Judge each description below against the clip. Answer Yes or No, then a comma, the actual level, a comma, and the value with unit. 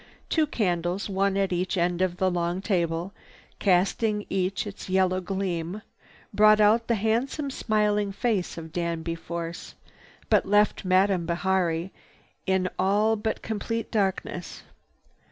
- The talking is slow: Yes, slow, 130 wpm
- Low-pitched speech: No, high, 190 Hz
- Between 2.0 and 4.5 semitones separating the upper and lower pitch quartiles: Yes, average, 2.9 semitones